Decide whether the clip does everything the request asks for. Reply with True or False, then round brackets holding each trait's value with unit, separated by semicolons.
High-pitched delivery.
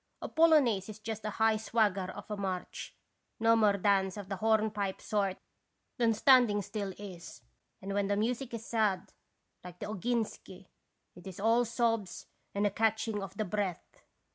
True (210 Hz)